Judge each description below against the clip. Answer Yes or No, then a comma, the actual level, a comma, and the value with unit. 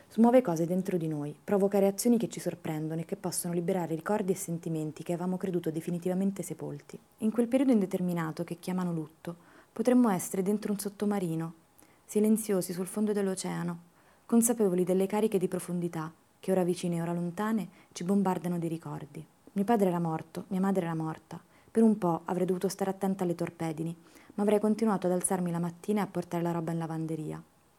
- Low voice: No, medium, 180 Hz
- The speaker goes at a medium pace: No, fast, 180 wpm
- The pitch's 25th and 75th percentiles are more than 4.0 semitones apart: No, average, 3.0 semitones